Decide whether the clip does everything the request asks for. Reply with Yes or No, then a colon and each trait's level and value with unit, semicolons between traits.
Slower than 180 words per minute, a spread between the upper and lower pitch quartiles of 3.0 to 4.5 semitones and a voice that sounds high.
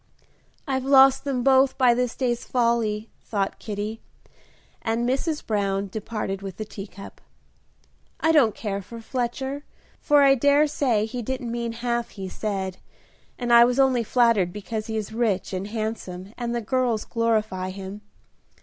Yes: average, 155 wpm; average, 3.4 semitones; high, 230 Hz